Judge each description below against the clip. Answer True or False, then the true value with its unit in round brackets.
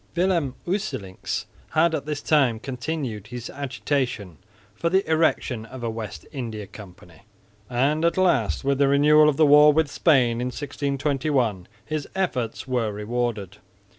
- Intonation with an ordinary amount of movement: True (5.0 semitones)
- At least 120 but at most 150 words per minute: True (145 wpm)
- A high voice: False (135 Hz)